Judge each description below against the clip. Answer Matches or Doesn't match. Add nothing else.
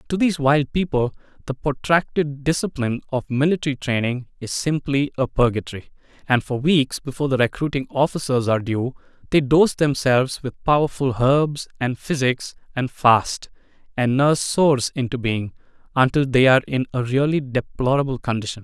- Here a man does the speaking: Matches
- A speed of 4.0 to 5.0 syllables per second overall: Doesn't match